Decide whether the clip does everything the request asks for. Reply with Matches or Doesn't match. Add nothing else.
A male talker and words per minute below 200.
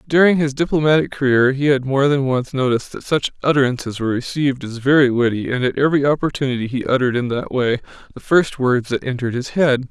Doesn't match